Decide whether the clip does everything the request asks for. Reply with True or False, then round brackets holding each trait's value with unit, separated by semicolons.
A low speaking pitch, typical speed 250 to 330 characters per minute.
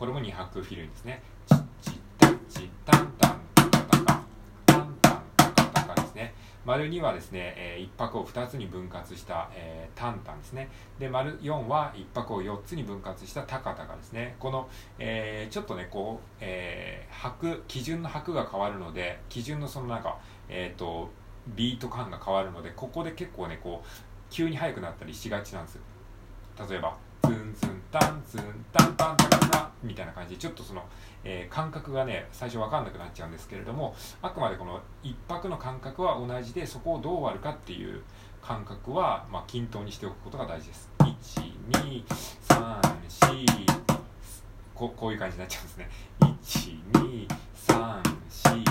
True (105 Hz; 290 characters per minute)